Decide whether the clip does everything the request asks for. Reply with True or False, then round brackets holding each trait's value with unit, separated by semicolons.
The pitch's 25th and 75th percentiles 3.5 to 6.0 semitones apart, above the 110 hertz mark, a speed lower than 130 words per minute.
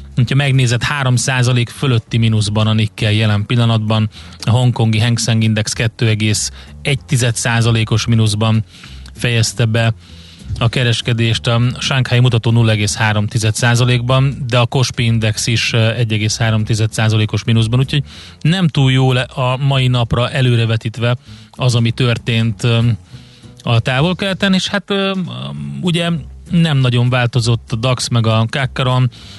False (2.5 semitones; 120 Hz; 110 wpm)